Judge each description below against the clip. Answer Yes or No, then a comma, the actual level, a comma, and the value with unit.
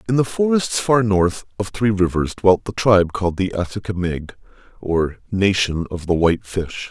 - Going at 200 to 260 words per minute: No, average, 175 wpm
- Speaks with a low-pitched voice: Yes, very low, 95 Hz